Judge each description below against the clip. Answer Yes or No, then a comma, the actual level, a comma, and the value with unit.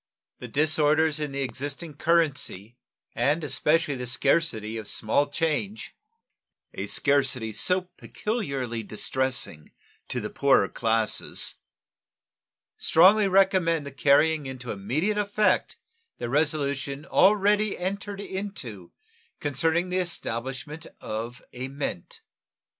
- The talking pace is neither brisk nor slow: No, slow, 105 wpm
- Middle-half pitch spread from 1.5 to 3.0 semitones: No, average, 5.0 semitones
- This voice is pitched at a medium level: Yes, medium, 145 Hz